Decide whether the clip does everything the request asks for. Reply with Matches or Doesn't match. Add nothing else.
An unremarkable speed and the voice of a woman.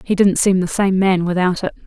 Doesn't match